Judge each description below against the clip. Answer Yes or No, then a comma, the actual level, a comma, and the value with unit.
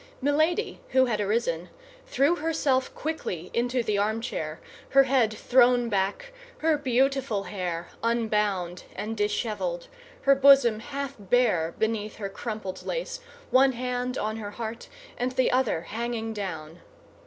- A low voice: No, high, 235 Hz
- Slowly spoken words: Yes, slow, 130 wpm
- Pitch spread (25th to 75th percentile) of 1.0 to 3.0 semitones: No, average, 4.3 semitones